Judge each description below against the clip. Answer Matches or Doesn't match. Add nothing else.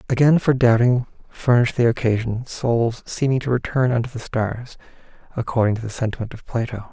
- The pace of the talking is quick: Doesn't match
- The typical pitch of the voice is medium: Doesn't match